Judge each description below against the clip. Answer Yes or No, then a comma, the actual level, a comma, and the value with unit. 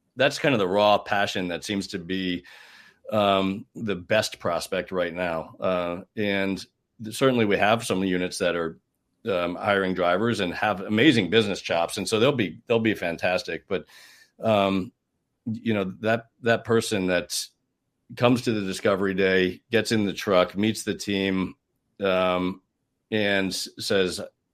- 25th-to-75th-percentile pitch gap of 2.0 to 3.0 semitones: Yes, average, 2.7 semitones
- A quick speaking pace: No, average, 155 wpm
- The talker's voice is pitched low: Yes, low, 100 Hz